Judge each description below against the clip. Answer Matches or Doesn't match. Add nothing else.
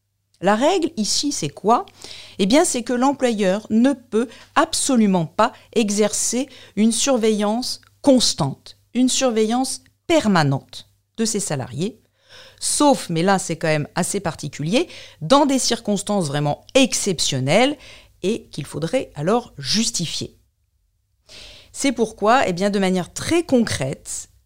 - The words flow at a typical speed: Doesn't match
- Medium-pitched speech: Doesn't match